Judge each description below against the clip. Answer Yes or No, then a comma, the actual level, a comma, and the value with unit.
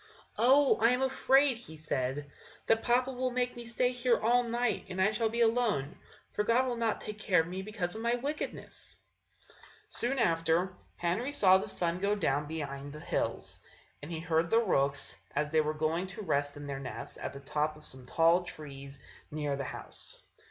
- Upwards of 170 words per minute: Yes, average, 195 wpm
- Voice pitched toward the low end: No, medium, 185 Hz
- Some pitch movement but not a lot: No, wide, 7.6 semitones